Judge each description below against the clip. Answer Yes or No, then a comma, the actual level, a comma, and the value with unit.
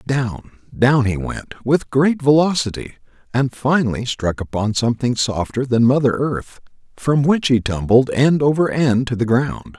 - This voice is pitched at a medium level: No, low, 130 Hz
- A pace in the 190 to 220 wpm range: No, average, 155 wpm